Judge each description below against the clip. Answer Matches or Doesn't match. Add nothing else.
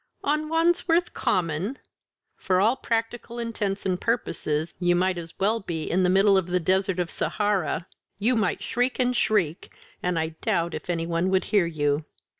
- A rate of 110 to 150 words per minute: Doesn't match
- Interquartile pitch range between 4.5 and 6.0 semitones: Matches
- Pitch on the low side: Doesn't match